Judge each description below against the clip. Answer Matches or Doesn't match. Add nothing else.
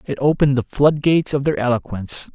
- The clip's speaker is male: Matches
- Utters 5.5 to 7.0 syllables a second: Matches